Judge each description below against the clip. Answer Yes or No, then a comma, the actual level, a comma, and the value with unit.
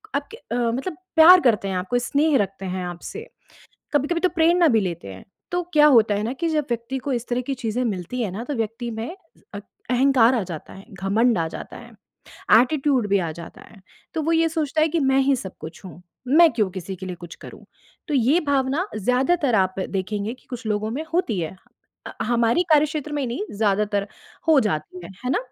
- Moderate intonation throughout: No, wide, 6.6 semitones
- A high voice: Yes, high, 240 Hz